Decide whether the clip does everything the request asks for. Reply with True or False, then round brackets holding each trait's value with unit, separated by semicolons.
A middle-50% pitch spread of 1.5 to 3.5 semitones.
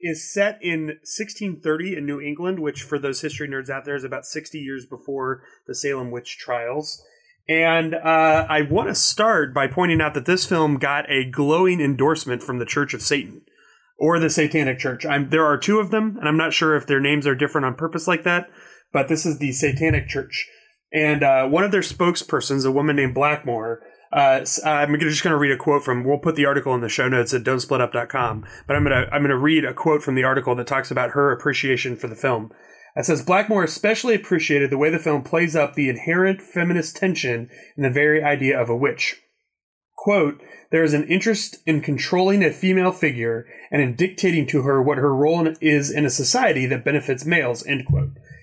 True (3.2 semitones)